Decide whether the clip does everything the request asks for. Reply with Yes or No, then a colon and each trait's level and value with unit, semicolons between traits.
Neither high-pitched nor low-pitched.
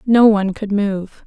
No: high, 205 Hz